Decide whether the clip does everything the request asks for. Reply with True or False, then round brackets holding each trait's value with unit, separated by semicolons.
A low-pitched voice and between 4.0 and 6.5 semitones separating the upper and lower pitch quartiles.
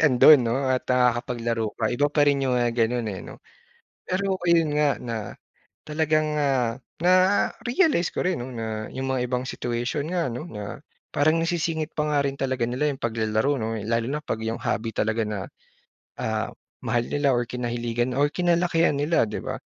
True (130 Hz; 4.5 semitones)